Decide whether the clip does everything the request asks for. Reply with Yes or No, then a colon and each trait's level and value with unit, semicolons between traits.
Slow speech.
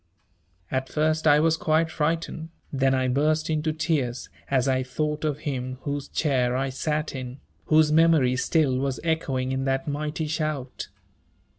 No: average, 155 wpm